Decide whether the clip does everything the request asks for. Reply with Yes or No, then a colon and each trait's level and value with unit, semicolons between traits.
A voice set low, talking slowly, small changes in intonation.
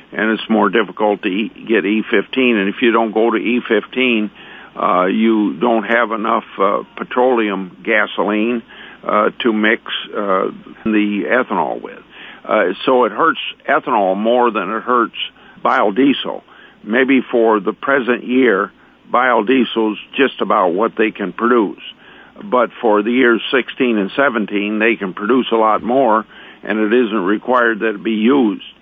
No: low, 115 Hz; average, 150 wpm; narrow, 2.1 semitones